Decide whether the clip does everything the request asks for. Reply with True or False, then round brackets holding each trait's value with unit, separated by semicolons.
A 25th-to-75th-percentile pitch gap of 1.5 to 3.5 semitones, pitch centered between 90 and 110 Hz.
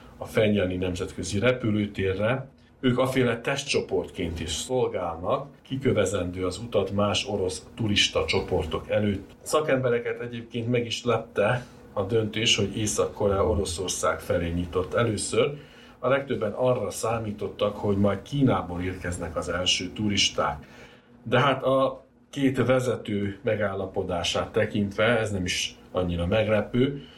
False (4.1 semitones; 105 Hz)